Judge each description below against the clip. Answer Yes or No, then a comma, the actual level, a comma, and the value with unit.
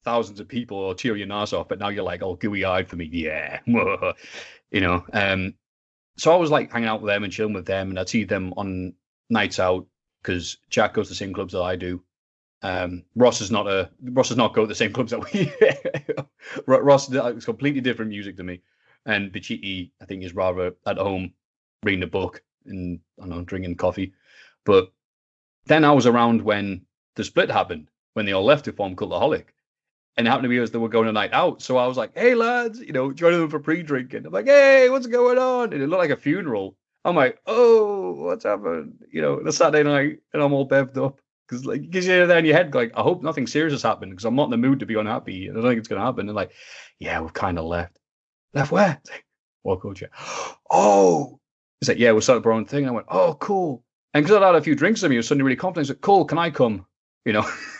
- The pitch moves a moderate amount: No, wide, 7.4 semitones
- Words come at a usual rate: No, fast, 250 wpm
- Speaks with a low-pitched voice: Yes, low, 115 Hz